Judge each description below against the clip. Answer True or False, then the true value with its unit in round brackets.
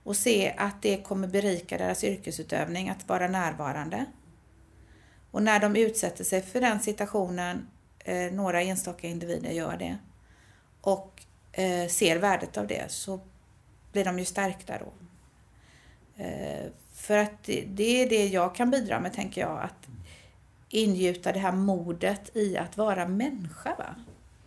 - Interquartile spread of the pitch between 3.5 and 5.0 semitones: False (2.9 semitones)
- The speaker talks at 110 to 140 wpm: True (135 wpm)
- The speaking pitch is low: False (195 Hz)